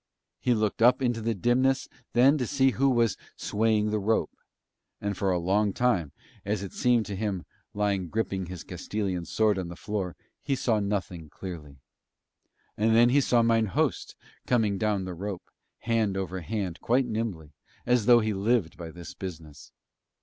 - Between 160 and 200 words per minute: Yes, average, 170 wpm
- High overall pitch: No, low, 105 Hz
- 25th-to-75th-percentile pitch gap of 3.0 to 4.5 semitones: Yes, average, 3.8 semitones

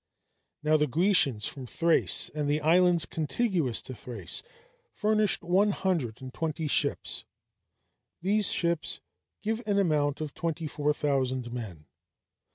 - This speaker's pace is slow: Yes, slow, 130 wpm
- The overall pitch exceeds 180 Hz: No, medium, 155 Hz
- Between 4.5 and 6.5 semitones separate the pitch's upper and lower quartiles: Yes, average, 5.1 semitones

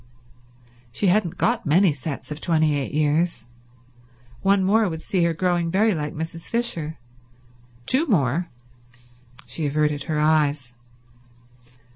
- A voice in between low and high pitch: Yes, medium, 160 Hz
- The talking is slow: Yes, slow, 125 wpm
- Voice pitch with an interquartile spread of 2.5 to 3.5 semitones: No, average, 3.9 semitones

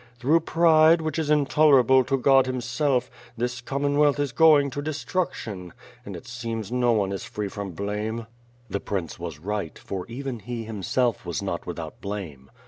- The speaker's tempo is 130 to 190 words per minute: Yes, average, 175 wpm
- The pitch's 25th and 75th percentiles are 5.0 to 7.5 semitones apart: Yes, wide, 5.5 semitones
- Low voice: Yes, low, 125 Hz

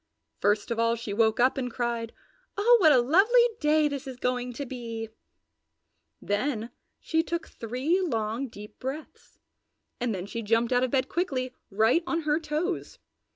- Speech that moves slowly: No, average, 165 wpm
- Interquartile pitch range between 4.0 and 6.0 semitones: Yes, average, 4.9 semitones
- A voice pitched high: Yes, very high, 250 Hz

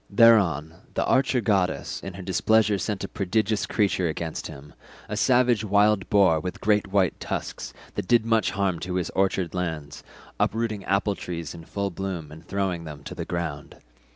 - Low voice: Yes, very low, 95 Hz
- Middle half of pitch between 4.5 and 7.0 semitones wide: No, average, 3.8 semitones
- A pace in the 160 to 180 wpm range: Yes, average, 170 wpm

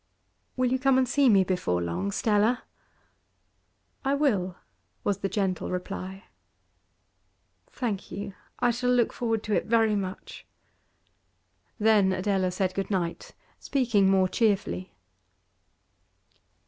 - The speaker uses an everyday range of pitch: Yes, average, 4.1 semitones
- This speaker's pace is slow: Yes, slow, 120 wpm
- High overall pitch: Yes, high, 200 Hz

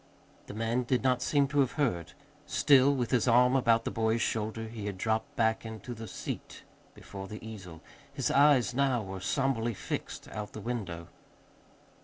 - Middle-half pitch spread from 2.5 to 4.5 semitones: Yes, average, 3.1 semitones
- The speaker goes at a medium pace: Yes, average, 175 wpm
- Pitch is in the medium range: No, low, 115 Hz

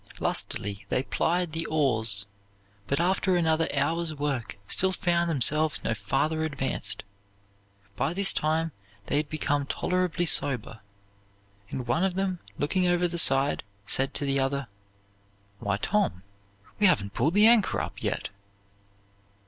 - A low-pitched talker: No, medium, 155 Hz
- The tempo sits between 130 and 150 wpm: Yes, average, 140 wpm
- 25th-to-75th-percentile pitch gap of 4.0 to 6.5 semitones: Yes, average, 4.6 semitones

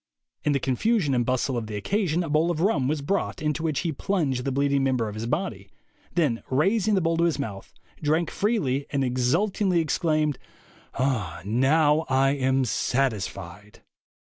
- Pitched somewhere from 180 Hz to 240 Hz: No, medium, 140 Hz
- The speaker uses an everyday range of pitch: Yes, average, 4.5 semitones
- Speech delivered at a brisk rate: No, average, 170 wpm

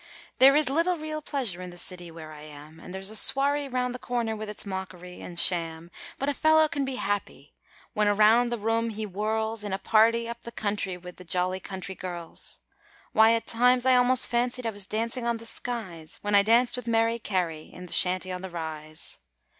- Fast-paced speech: Yes, fast, 210 wpm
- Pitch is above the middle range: Yes, high, 215 Hz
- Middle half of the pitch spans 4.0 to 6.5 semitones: Yes, average, 5.0 semitones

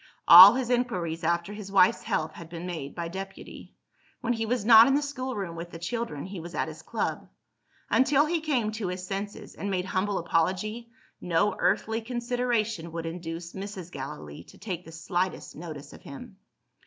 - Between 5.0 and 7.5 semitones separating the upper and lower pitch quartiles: Yes, average, 5.3 semitones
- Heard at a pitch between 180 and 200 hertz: Yes, high, 190 Hz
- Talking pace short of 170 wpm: No, average, 180 wpm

